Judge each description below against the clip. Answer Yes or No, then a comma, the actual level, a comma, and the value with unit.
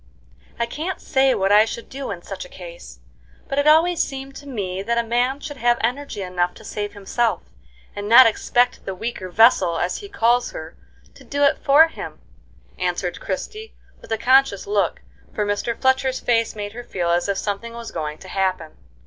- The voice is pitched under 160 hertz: No, high, 235 Hz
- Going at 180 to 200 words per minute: Yes, average, 195 wpm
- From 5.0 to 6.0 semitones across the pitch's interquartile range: Yes, average, 5.3 semitones